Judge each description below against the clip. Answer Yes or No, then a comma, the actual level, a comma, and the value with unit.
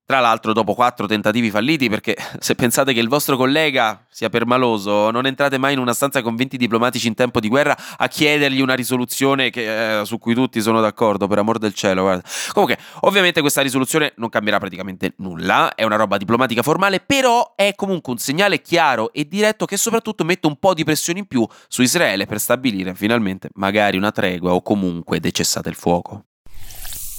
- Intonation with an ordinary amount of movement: Yes, average, 5.0 semitones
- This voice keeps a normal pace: No, fast, 195 wpm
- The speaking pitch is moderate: No, low, 120 Hz